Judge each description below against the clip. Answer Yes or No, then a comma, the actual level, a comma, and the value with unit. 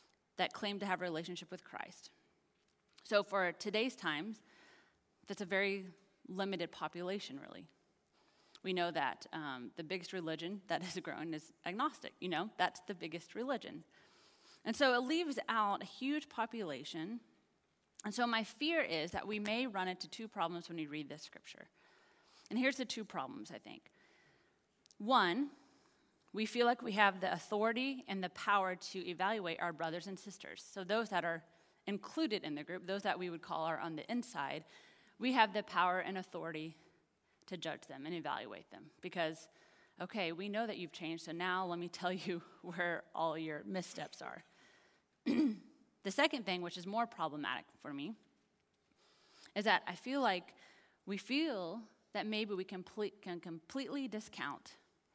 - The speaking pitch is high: Yes, high, 195 Hz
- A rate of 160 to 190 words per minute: Yes, average, 170 wpm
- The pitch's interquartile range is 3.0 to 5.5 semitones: Yes, average, 4.7 semitones